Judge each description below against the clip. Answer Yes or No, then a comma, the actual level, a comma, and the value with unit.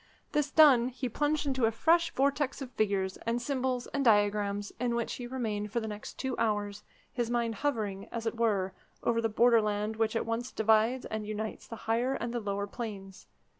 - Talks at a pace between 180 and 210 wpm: Yes, average, 195 wpm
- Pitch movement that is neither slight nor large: Yes, average, 3.1 semitones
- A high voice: Yes, high, 230 Hz